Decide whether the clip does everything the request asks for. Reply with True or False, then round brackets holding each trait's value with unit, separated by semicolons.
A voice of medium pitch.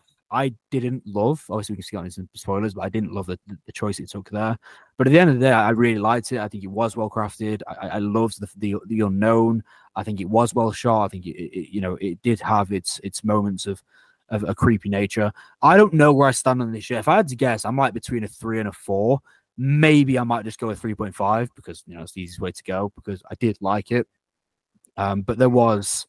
False (110 Hz)